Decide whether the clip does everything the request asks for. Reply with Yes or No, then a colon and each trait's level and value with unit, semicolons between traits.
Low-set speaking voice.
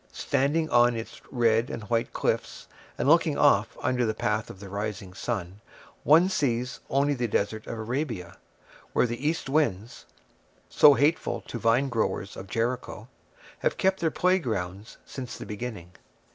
Yes: low, 120 Hz